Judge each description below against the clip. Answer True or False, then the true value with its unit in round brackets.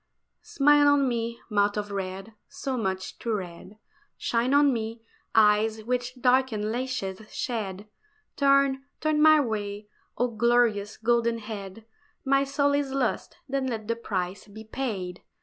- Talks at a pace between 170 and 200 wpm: False (140 wpm)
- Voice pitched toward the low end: False (230 Hz)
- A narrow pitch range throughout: False (4.3 semitones)